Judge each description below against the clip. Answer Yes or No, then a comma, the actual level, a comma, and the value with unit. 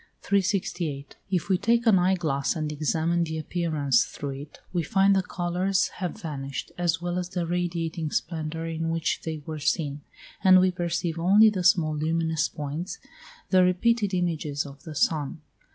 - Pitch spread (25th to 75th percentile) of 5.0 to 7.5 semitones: No, average, 2.9 semitones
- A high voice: No, medium, 170 Hz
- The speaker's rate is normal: Yes, average, 170 wpm